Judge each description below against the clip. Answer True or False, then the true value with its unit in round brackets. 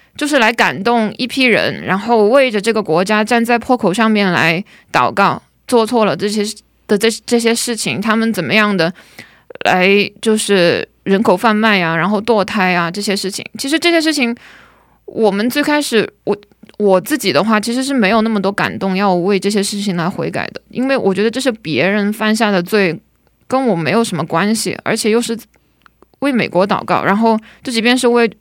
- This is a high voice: True (215 Hz)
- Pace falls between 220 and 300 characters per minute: True (285 characters per minute)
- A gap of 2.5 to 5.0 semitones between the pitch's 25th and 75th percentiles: True (3.2 semitones)